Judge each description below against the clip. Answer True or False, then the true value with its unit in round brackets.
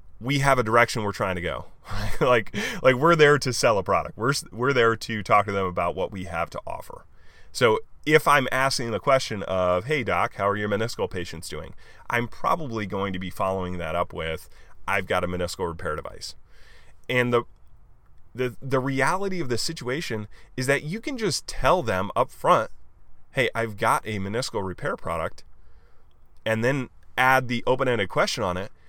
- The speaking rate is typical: True (190 wpm)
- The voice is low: True (115 Hz)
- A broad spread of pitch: True (6.4 semitones)